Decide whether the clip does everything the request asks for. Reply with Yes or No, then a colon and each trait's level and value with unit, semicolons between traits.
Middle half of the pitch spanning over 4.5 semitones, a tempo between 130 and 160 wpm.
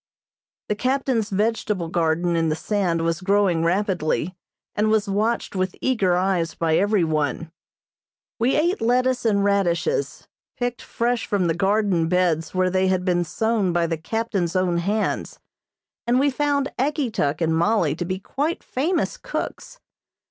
Yes: average, 5.1 semitones; average, 150 wpm